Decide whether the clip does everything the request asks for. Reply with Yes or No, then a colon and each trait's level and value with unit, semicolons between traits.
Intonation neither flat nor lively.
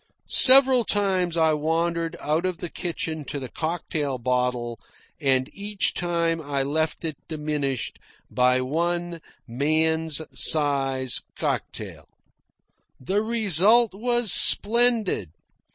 Yes: average, 4.8 semitones